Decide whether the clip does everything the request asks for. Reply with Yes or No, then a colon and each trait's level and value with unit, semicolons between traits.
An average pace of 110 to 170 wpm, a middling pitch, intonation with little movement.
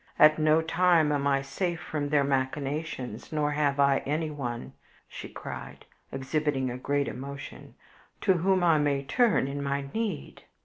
Yes: average, 150 wpm; medium, 145 Hz; narrow, 2.3 semitones